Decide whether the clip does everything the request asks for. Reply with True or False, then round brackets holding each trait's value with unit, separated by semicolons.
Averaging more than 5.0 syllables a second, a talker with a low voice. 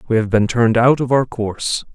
True (5.9 syllables/s; 120 Hz)